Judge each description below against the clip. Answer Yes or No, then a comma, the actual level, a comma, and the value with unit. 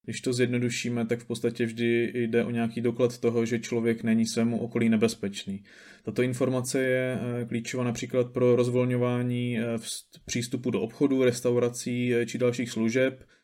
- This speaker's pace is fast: No, average, 145 wpm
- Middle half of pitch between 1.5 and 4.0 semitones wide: No, narrow, 1.1 semitones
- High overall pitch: No, low, 120 Hz